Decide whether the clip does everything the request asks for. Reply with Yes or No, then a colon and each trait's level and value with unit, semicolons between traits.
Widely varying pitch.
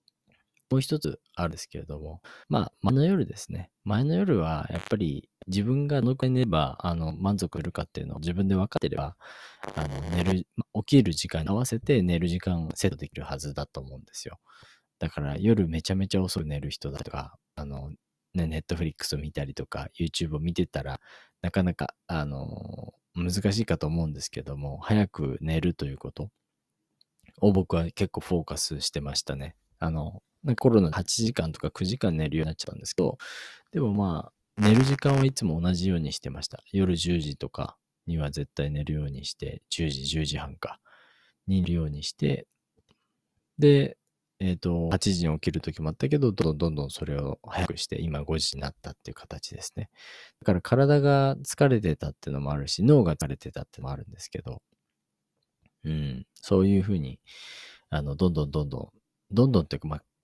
No: average, 4.8 semitones